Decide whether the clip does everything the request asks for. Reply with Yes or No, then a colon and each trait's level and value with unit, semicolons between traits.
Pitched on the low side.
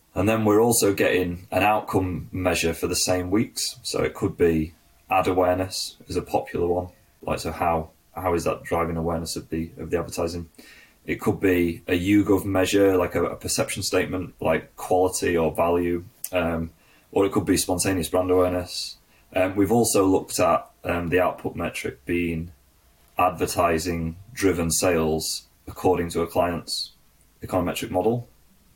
Yes: very low, 90 Hz